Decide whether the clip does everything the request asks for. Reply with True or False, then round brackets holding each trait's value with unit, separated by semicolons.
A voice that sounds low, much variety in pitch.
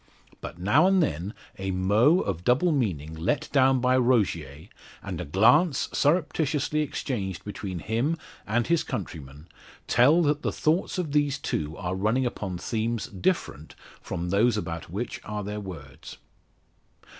True (110 Hz; 7.6 semitones)